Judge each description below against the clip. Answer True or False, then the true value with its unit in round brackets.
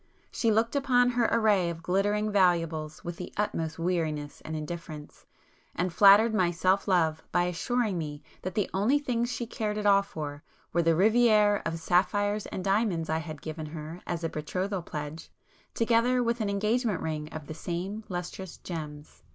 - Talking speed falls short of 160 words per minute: False (175 wpm)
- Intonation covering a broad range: False (4.7 semitones)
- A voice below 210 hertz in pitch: True (185 Hz)